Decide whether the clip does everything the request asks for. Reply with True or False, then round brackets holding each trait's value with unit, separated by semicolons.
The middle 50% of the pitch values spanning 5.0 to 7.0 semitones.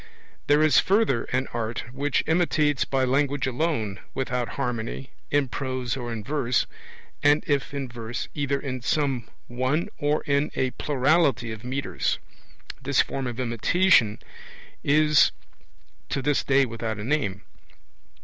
False (3.3 semitones)